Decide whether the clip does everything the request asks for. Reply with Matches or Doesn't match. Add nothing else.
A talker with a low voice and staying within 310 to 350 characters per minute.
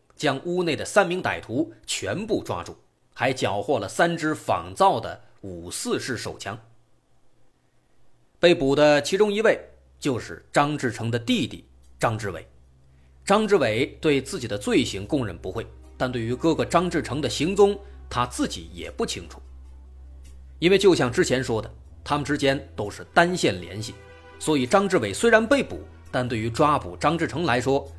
Doesn't match